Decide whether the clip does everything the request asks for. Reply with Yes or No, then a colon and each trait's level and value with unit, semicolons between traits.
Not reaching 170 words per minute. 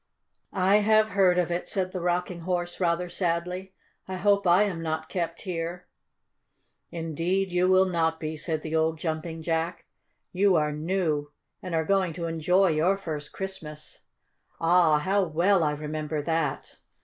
Yes: average, 160 wpm